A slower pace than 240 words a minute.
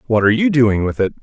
No: fast, 295 wpm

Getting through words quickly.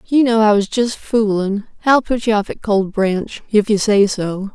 Yes: fast, 225 wpm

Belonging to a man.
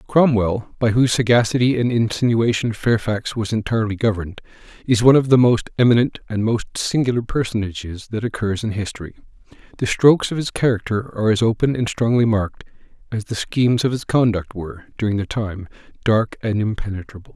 Yes: male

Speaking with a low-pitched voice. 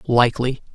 Yes: low, 125 Hz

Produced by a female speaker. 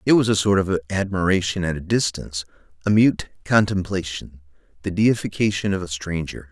No: male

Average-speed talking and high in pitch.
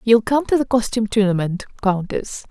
Yes: average, 170 wpm; high, 220 Hz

